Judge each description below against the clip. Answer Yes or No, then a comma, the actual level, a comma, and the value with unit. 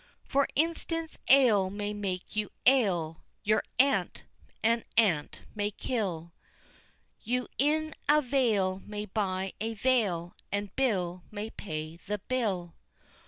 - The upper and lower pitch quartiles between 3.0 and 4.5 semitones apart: No, average, 5.2 semitones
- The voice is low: No, high, 210 Hz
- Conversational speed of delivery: No, slow, 120 wpm